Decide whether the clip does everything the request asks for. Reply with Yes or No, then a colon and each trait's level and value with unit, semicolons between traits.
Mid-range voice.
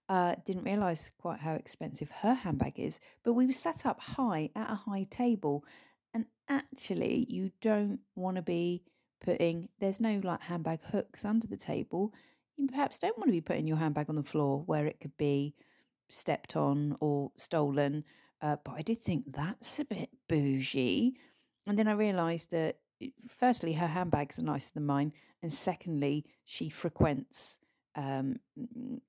Yes: medium, 175 Hz